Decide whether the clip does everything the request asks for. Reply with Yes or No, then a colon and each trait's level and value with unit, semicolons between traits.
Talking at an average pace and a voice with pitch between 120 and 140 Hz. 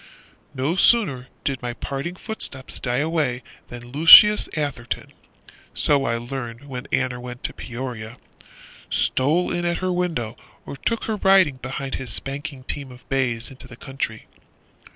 Yes: average, 150 wpm; low, 135 Hz